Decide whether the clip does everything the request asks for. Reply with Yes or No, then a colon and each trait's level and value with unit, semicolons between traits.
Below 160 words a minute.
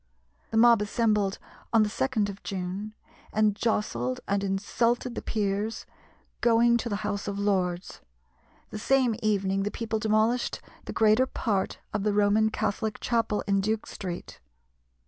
Yes: average, 145 wpm